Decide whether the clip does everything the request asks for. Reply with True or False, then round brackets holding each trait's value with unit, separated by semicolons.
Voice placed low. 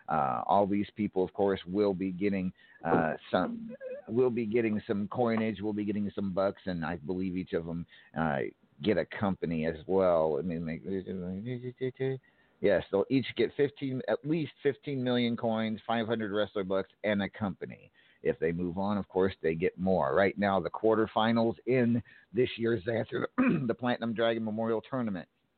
True (110 Hz)